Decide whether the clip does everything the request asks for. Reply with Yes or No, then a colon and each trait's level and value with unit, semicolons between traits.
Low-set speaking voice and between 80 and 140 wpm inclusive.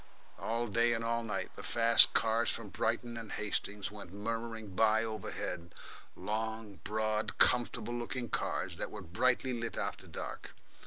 No: low, 110 Hz; average, 150 wpm